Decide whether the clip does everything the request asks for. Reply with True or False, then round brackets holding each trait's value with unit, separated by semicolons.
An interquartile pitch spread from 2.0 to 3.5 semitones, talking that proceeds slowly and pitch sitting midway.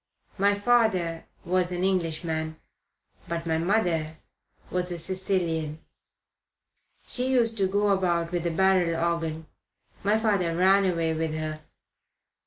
True (2.9 semitones; 125 wpm; 175 Hz)